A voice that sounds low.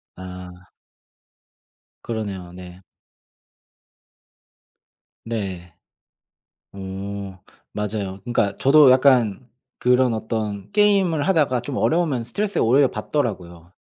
Yes: low, 110 Hz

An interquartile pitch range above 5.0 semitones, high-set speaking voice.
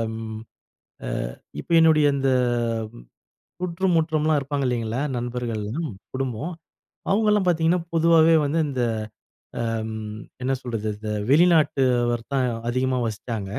No: wide, 5.6 semitones; low, 135 Hz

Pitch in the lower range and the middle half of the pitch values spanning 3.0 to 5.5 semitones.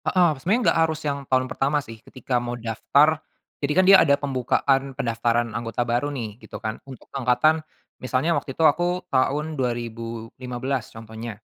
Yes: low, 130 Hz; average, 4.0 semitones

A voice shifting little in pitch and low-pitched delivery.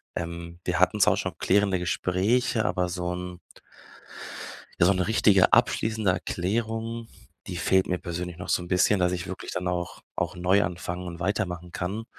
Yes: narrow, 2.2 semitones; very low, 90 Hz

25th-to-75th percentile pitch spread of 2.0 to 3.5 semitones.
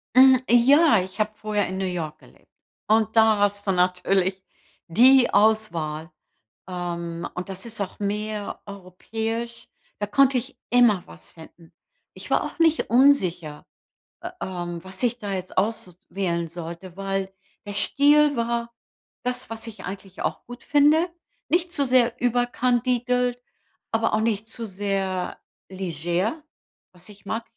No: average, 4.7 semitones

